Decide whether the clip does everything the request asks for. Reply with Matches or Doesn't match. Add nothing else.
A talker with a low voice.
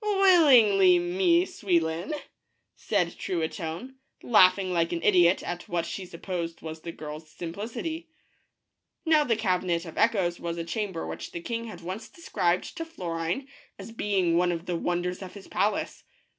Doesn't match